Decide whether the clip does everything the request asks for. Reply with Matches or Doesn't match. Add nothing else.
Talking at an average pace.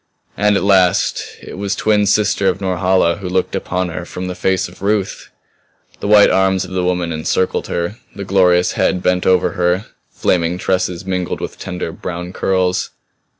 Matches